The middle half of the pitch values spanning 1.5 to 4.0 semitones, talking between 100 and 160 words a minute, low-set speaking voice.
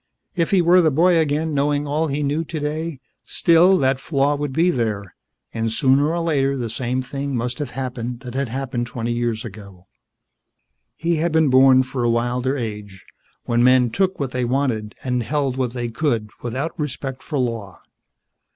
No: average, 3.7 semitones; average, 180 wpm; low, 130 Hz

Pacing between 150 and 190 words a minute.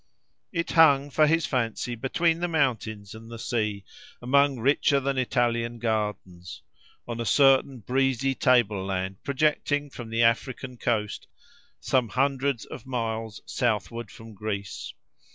No: slow, 135 wpm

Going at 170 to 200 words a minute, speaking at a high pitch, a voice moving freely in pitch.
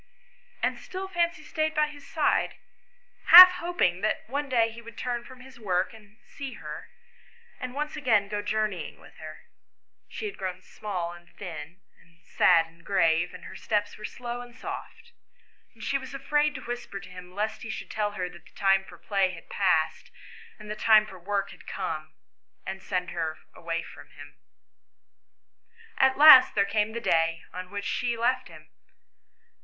Yes: average, 180 wpm; high, 210 Hz; wide, 5.9 semitones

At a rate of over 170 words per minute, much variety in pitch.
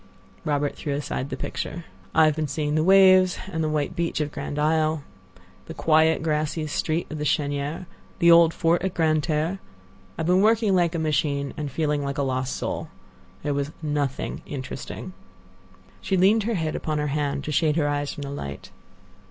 No: average, 185 wpm; narrow, 2.5 semitones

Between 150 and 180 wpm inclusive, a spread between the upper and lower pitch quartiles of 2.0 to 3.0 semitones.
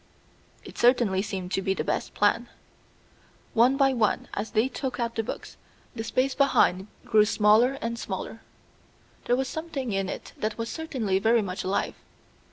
No: average, 170 wpm; average, 4.1 semitones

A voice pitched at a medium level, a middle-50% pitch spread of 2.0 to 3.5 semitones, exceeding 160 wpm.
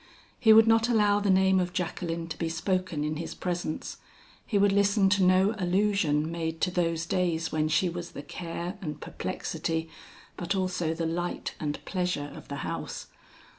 Yes: medium, 175 Hz; average, 2.9 semitones; average, 175 wpm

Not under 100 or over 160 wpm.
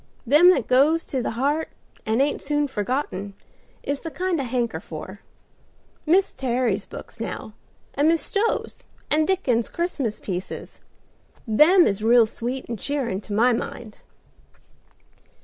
Yes: average, 140 wpm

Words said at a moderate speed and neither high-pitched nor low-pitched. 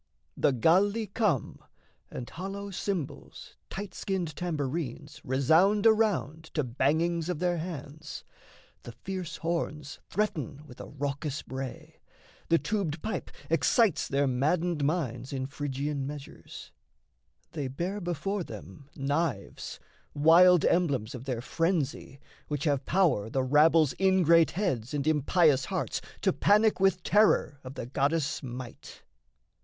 No: slow, 125 wpm; medium, 155 Hz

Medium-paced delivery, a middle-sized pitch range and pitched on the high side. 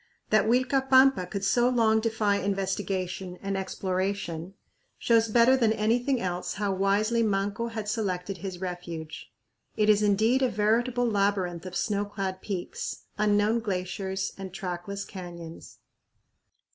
No: slow, 130 wpm; average, 3.0 semitones; high, 200 Hz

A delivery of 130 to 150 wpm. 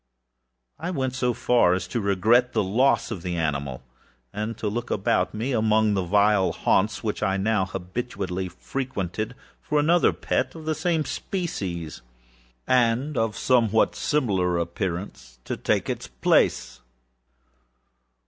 Yes: average, 145 wpm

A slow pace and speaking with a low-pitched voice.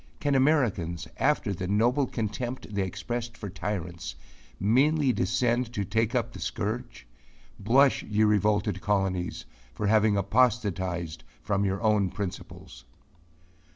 Yes: slow, 120 wpm; low, 105 Hz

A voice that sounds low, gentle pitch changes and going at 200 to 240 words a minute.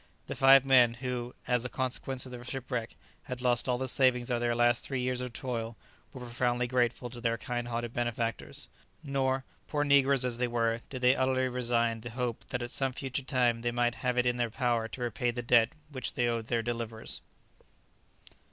Yes: low, 120 Hz; narrow, 1.3 semitones; fast, 205 wpm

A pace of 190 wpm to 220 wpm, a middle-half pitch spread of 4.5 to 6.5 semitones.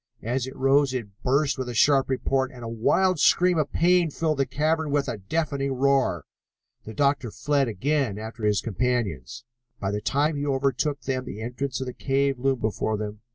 No: average, 195 wpm; average, 3.7 semitones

